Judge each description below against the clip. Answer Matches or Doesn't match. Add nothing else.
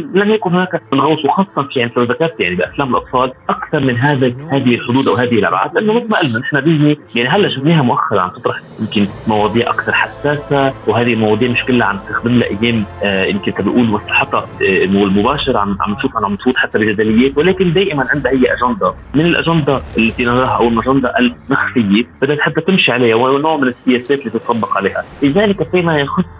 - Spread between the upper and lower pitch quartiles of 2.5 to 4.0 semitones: Doesn't match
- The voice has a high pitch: Doesn't match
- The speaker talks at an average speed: Doesn't match